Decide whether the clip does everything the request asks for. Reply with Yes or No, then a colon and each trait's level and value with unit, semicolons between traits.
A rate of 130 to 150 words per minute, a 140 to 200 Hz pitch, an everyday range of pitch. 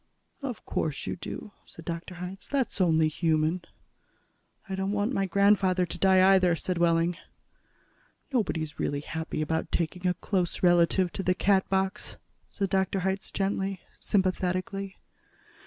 No: average, 140 wpm; medium, 185 Hz; narrow, 2.3 semitones